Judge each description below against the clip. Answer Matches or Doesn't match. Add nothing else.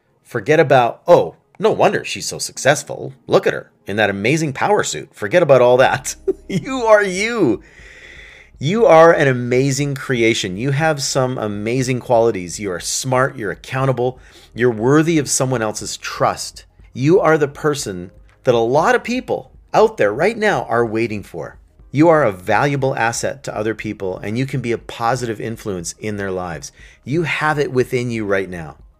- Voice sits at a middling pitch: Doesn't match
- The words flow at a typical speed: Matches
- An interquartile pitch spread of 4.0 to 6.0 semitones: Matches